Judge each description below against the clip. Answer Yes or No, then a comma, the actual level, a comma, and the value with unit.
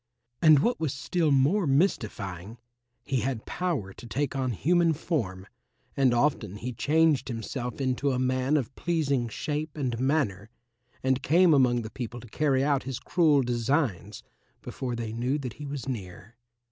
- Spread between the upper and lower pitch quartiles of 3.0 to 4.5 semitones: Yes, average, 4.0 semitones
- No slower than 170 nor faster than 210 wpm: No, average, 160 wpm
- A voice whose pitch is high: No, low, 130 Hz